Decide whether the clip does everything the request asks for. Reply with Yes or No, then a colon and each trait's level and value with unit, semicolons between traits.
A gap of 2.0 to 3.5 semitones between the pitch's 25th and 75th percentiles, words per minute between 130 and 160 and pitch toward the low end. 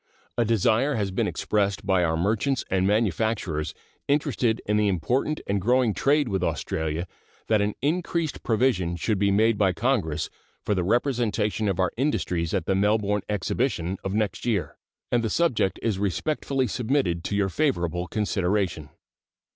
No: average, 4.4 semitones; average, 155 wpm; low, 105 Hz